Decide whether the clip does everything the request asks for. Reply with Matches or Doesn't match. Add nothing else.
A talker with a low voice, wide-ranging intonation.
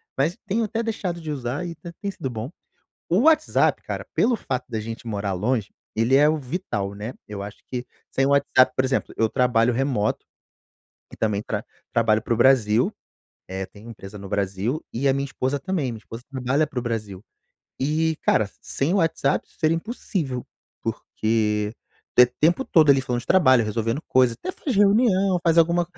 Matches